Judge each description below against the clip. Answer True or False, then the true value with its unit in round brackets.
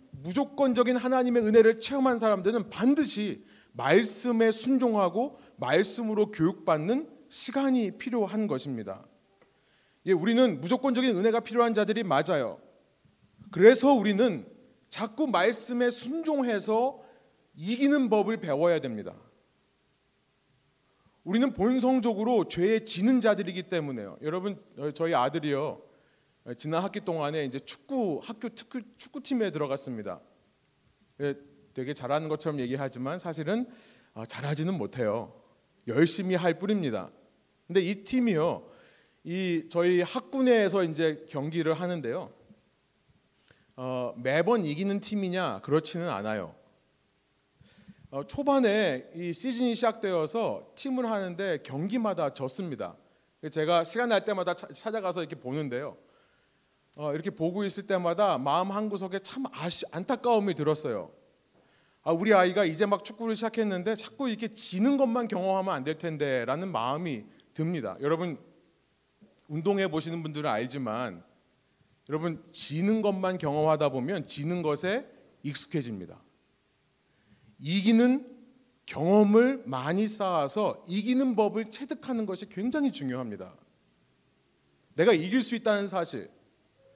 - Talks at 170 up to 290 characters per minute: True (280 characters per minute)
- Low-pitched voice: False (195 Hz)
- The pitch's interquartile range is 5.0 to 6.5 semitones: False (7.0 semitones)